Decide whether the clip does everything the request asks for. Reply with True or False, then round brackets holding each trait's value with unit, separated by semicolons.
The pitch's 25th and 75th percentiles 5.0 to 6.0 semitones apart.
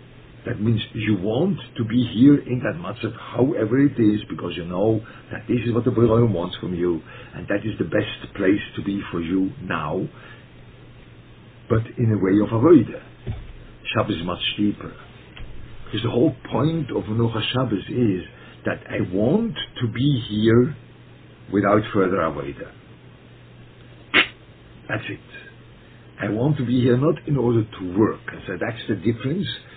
False (3.0 semitones)